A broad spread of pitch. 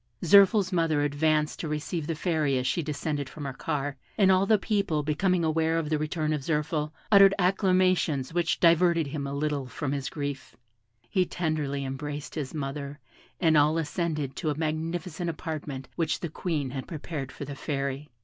No: average, 2.9 semitones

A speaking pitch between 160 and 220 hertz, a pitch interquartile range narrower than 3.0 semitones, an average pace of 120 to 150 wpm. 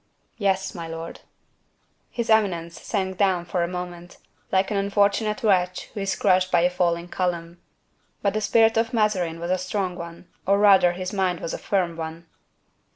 No: medium, 185 Hz; narrow, 2.5 semitones; average, 175 wpm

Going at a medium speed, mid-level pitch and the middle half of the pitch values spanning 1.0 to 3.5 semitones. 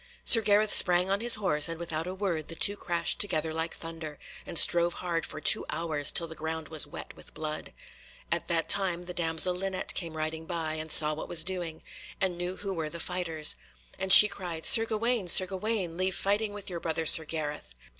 No: fast, 210 wpm; medium, 170 Hz; average, 2.9 semitones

